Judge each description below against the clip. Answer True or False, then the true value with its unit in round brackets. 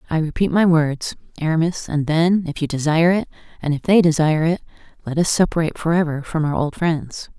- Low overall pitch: False (160 Hz)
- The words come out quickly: False (195 wpm)